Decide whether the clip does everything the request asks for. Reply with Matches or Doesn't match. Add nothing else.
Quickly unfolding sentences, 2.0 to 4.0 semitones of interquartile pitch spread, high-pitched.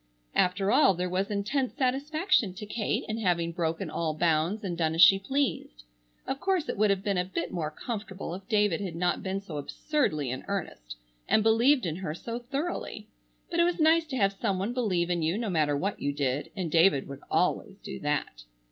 Doesn't match